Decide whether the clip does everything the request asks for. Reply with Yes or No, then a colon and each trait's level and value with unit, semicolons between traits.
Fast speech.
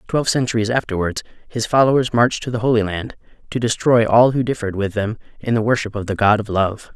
Yes: fast, 215 wpm